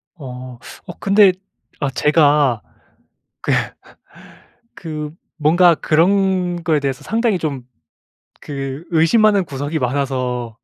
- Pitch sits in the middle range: Yes, medium, 150 Hz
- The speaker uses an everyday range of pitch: Yes, average, 4.8 semitones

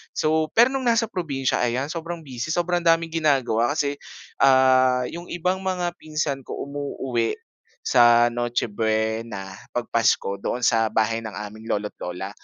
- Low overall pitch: Yes, low, 130 Hz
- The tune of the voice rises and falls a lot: Yes, wide, 6.0 semitones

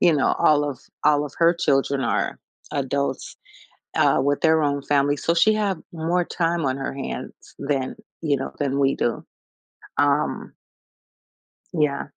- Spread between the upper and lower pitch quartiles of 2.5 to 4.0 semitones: Yes, average, 2.9 semitones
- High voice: No, medium, 145 Hz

